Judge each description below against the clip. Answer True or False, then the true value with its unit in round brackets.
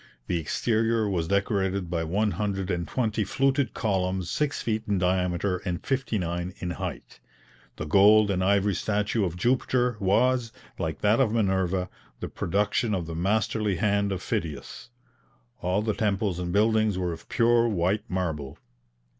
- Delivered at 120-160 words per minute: True (155 wpm)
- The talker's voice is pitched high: False (100 Hz)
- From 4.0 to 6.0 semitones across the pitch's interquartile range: False (3.3 semitones)